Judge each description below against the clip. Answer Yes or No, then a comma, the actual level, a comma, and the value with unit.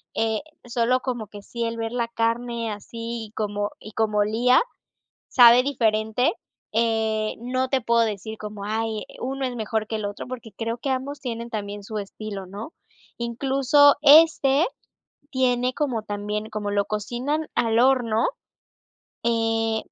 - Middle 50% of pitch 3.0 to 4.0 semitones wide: No, narrow, 2.6 semitones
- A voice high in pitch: Yes, high, 230 Hz